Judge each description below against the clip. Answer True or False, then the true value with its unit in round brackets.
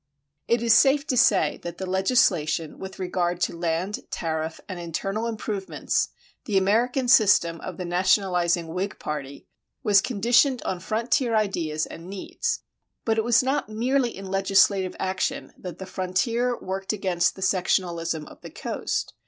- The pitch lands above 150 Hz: True (190 Hz)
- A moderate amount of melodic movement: True (4.5 semitones)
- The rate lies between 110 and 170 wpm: True (155 wpm)